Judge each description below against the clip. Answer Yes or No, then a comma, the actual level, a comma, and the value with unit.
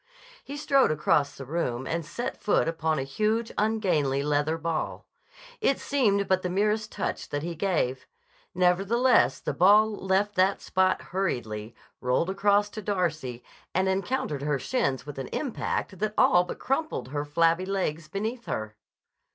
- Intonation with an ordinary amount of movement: No, wide, 5.9 semitones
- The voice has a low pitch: No, medium, 180 Hz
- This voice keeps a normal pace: Yes, average, 155 wpm